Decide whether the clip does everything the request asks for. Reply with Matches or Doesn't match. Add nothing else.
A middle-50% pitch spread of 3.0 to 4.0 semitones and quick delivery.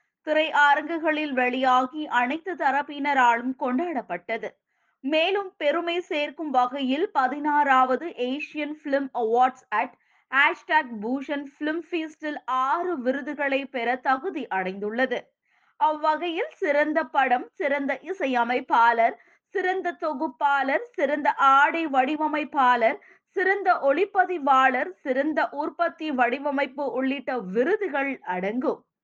Doesn't match